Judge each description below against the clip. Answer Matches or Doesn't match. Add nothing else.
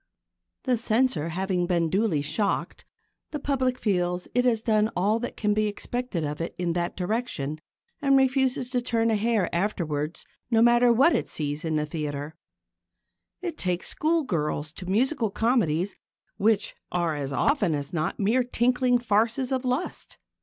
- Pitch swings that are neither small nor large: Doesn't match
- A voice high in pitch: Matches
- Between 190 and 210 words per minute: Doesn't match